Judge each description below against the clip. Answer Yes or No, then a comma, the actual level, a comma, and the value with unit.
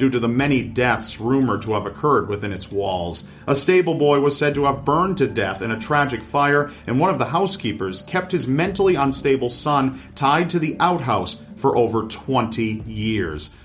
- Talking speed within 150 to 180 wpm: No, average, 195 wpm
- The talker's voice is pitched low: Yes, low, 130 Hz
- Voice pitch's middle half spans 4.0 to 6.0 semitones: Yes, average, 4.8 semitones